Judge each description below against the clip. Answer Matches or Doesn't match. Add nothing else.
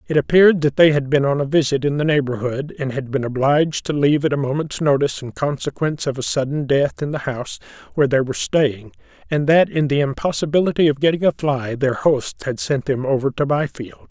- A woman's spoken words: Doesn't match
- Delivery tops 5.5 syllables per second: Matches